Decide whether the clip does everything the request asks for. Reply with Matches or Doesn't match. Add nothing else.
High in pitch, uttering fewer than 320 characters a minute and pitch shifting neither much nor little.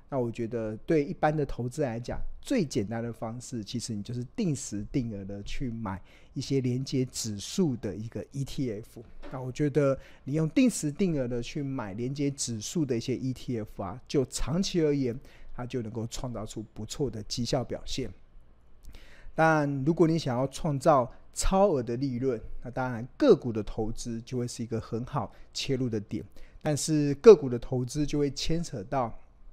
Doesn't match